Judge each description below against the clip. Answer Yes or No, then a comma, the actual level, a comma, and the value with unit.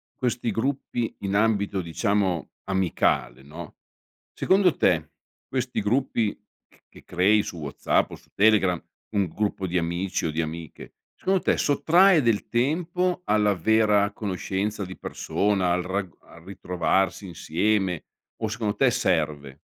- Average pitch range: Yes, average, 4.1 semitones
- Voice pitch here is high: No, low, 100 Hz